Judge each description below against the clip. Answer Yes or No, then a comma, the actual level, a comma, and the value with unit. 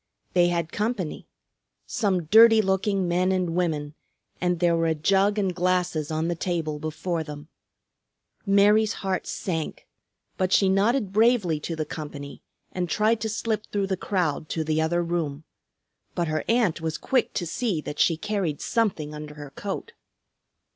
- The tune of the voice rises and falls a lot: No, average, 4.2 semitones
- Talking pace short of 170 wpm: Yes, average, 160 wpm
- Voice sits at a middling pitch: Yes, medium, 175 Hz